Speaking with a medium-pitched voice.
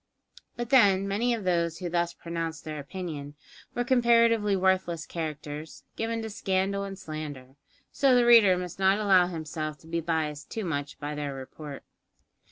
Yes: medium, 175 Hz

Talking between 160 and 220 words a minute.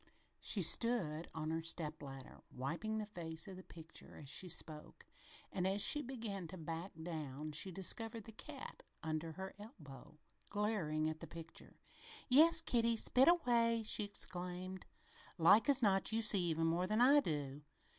Yes: average, 165 wpm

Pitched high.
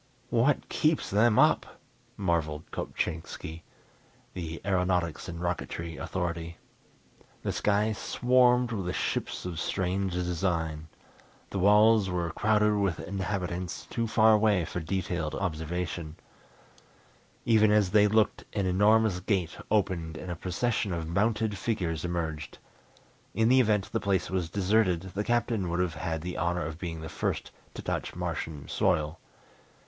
No: very low, 90 Hz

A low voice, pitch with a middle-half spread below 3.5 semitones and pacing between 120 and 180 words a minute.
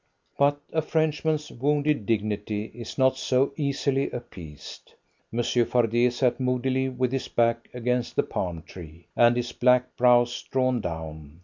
Yes: low, 125 Hz; average, 3.0 semitones; average, 140 wpm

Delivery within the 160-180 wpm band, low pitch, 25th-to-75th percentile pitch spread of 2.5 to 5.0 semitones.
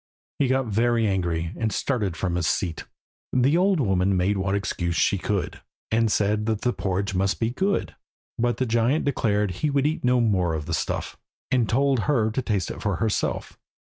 No: average, 195 wpm; low, 110 Hz; average, 4.7 semitones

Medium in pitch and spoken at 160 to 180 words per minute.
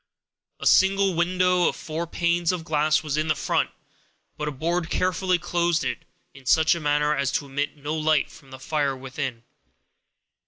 Yes: medium, 155 Hz; average, 170 wpm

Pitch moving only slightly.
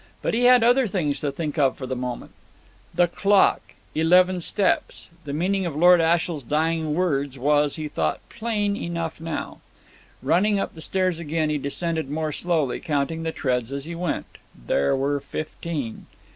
No: average, 3.8 semitones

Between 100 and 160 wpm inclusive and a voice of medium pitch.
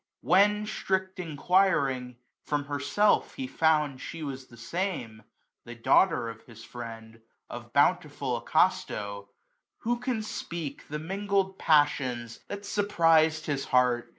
Yes: slow, 135 wpm; medium, 150 Hz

